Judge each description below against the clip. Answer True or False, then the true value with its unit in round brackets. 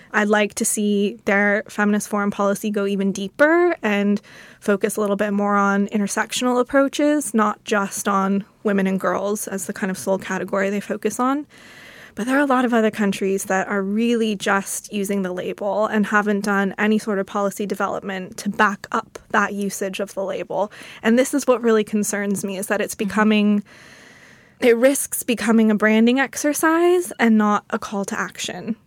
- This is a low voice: False (210 Hz)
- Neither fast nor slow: True (185 wpm)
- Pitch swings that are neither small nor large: False (1.9 semitones)